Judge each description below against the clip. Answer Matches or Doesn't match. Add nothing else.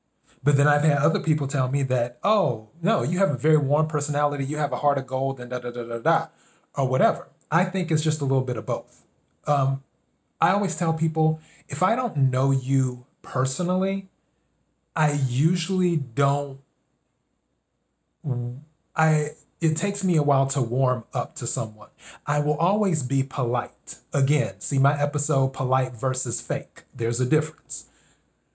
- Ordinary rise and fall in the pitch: Matches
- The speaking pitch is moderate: Matches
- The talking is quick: Doesn't match